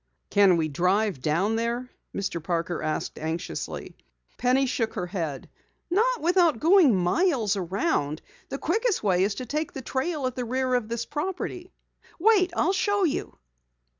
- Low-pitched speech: No, high, 240 Hz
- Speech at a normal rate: Yes, average, 155 wpm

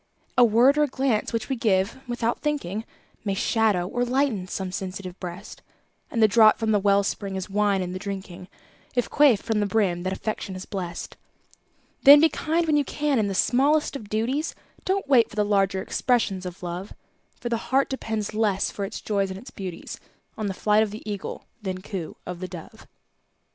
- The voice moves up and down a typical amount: Yes, average, 4.2 semitones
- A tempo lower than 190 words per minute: No, average, 200 wpm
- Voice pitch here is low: No, high, 210 Hz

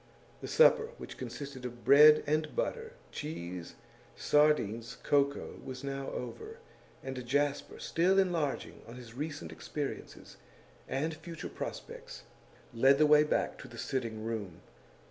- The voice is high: No, medium, 140 Hz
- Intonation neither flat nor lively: Yes, average, 4.1 semitones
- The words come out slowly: Yes, slow, 130 wpm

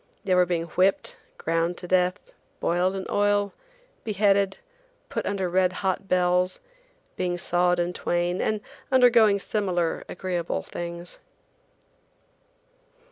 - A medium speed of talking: No, slow, 115 wpm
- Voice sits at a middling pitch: Yes, medium, 180 Hz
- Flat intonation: Yes, narrow, 2.1 semitones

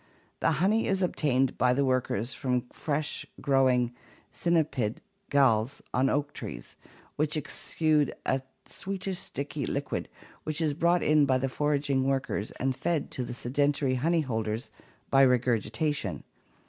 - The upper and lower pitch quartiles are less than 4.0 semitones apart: Yes, average, 3.2 semitones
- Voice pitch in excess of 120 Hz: Yes, low, 135 Hz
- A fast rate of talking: No, slow, 135 wpm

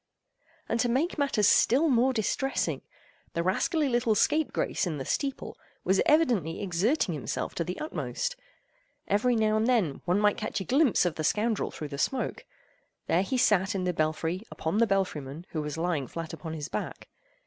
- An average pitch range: No, wide, 6.9 semitones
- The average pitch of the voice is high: Yes, high, 200 Hz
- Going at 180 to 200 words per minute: Yes, average, 185 wpm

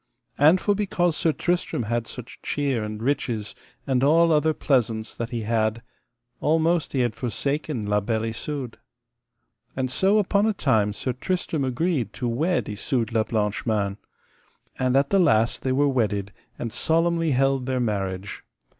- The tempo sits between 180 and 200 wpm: No, average, 160 wpm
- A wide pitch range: Yes, wide, 5.9 semitones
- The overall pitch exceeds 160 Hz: No, low, 130 Hz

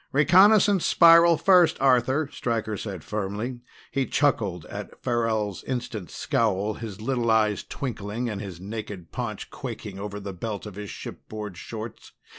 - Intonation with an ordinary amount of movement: Yes, average, 4.2 semitones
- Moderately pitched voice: No, low, 110 Hz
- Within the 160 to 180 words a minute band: No, average, 140 wpm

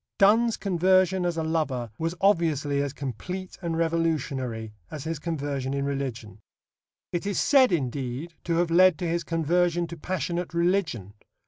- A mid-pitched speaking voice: Yes, medium, 165 Hz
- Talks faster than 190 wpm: No, average, 150 wpm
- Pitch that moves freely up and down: No, average, 4.1 semitones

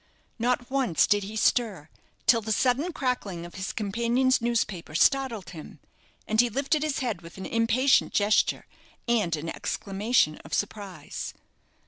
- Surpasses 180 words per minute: No, average, 145 wpm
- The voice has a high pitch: Yes, high, 225 Hz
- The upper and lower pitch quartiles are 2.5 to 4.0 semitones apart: No, average, 4.5 semitones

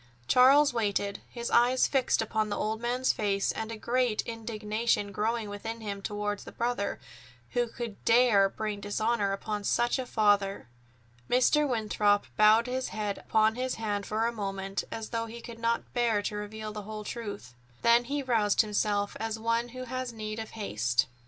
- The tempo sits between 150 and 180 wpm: Yes, average, 175 wpm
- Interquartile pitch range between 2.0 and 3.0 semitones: Yes, narrow, 2.4 semitones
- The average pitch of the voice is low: No, high, 220 Hz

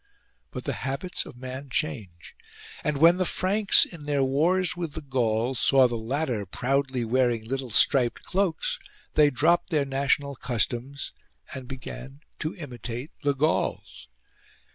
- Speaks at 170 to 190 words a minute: No, average, 140 wpm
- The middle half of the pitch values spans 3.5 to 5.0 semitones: Yes, average, 3.9 semitones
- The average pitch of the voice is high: No, low, 135 Hz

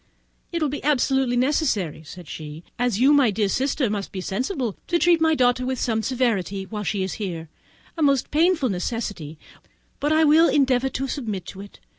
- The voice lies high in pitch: Yes, high, 245 Hz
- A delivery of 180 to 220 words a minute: Yes, average, 190 wpm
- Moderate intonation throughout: No, wide, 6.4 semitones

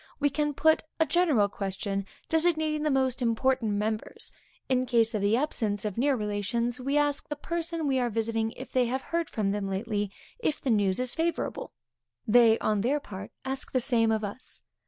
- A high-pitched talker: Yes, high, 240 Hz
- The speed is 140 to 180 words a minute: No, average, 190 wpm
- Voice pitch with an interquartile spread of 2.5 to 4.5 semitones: No, wide, 5.4 semitones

